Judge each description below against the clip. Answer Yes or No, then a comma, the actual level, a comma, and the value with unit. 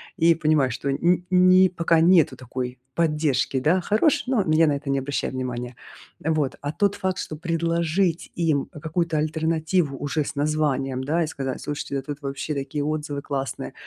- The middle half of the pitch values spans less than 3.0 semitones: No, average, 3.3 semitones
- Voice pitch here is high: No, medium, 155 Hz